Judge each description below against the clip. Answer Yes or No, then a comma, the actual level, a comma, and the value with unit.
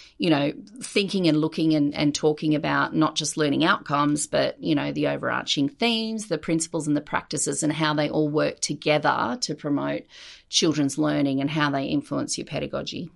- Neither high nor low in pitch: Yes, medium, 155 Hz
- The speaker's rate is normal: Yes, average, 185 wpm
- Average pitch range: No, narrow, 1.8 semitones